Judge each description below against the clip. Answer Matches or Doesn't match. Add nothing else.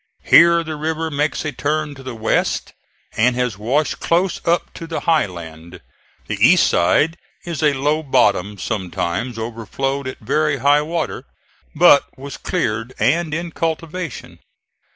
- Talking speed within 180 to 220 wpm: Doesn't match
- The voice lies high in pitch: Doesn't match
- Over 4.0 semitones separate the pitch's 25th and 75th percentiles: Matches